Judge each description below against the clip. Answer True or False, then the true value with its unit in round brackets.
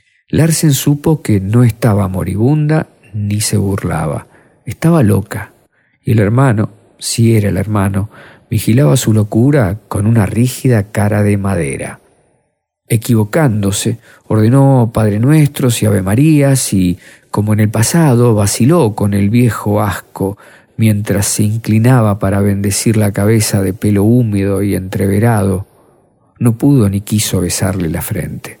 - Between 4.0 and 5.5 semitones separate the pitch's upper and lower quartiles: False (3.5 semitones)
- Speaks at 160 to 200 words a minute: False (130 wpm)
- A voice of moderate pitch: False (110 Hz)